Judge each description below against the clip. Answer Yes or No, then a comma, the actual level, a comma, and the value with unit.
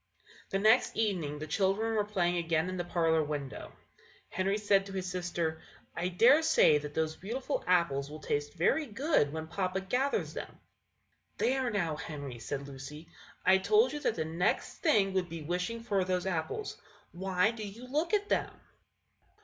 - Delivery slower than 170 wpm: No, average, 175 wpm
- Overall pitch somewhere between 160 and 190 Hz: Yes, medium, 185 Hz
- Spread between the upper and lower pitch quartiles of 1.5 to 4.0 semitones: No, average, 5.3 semitones